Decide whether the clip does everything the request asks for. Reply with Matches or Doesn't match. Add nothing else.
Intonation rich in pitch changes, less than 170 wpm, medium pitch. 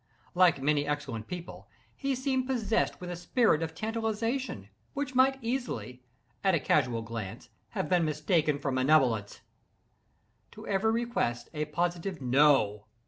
Matches